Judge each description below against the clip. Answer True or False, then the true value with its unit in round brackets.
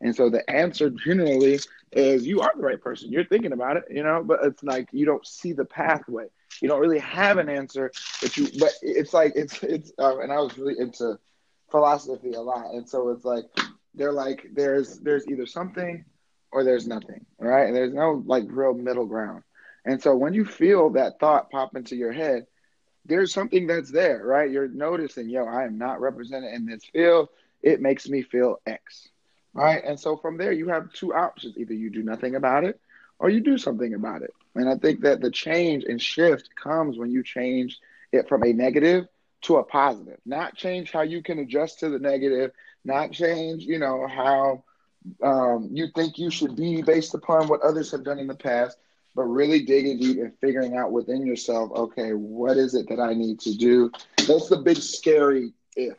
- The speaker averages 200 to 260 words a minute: True (205 wpm)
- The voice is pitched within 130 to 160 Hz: True (135 Hz)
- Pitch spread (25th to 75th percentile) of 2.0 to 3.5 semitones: False (4.2 semitones)